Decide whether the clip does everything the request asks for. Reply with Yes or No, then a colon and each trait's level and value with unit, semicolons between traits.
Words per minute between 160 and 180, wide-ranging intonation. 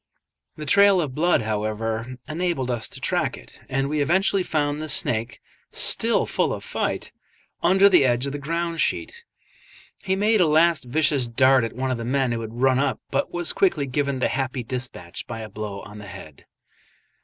No: average, 190 wpm; wide, 5.8 semitones